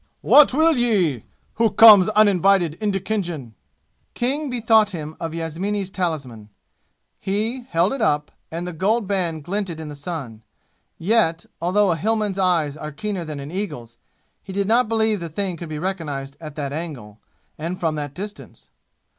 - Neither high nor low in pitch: Yes, medium, 180 Hz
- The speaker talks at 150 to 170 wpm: Yes, average, 165 wpm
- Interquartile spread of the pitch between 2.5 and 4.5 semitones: No, average, 5.2 semitones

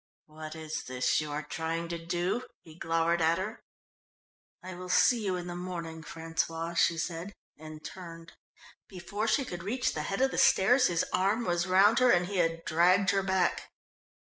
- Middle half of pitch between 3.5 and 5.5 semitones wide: No, narrow, 2.6 semitones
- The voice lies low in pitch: No, medium, 175 Hz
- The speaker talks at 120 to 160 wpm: No, average, 185 wpm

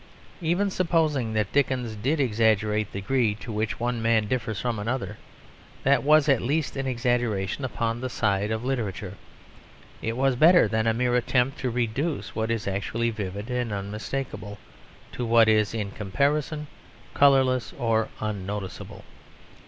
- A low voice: Yes, low, 115 Hz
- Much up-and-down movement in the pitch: No, average, 3.8 semitones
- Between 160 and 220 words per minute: No, average, 150 wpm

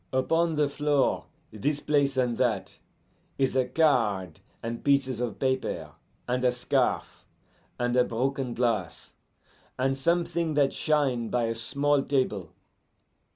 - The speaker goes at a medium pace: No, slow, 130 wpm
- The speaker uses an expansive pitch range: No, average, 3.3 semitones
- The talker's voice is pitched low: Yes, low, 130 Hz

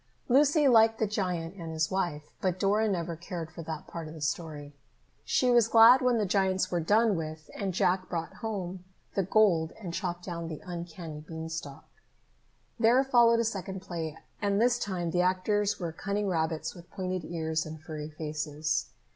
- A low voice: No, medium, 180 Hz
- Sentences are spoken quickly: No, average, 180 wpm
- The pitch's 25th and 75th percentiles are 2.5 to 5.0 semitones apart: Yes, average, 4.3 semitones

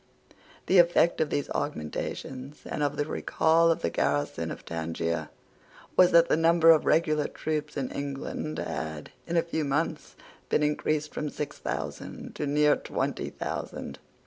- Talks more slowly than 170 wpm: Yes, average, 155 wpm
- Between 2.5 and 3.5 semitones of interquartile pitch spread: Yes, average, 2.9 semitones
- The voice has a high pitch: No, medium, 150 Hz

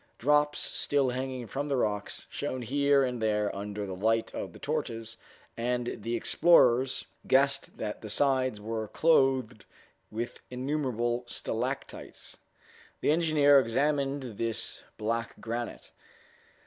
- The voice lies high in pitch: No, low, 125 Hz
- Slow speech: Yes, slow, 120 wpm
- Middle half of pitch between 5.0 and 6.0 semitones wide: No, average, 3.5 semitones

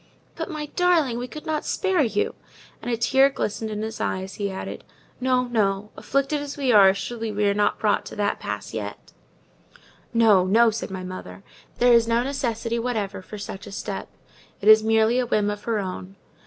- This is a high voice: Yes, high, 225 Hz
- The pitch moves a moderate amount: Yes, average, 3.6 semitones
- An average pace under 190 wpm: No, average, 195 wpm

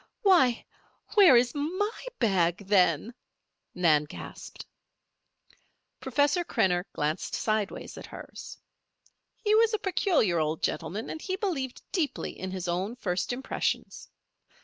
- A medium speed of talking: No, slow, 125 wpm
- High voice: Yes, high, 235 Hz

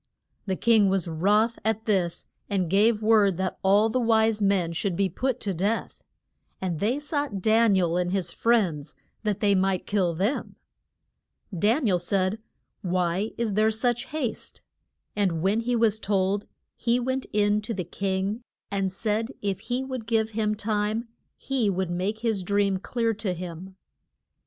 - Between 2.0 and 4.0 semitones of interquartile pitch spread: Yes, average, 3.0 semitones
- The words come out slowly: No, average, 170 wpm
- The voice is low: No, high, 205 Hz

